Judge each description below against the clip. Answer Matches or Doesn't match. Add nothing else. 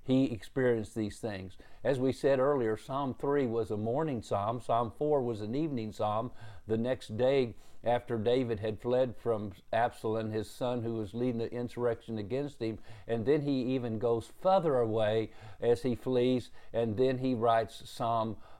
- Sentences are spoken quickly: Doesn't match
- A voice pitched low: Matches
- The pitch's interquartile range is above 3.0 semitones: Doesn't match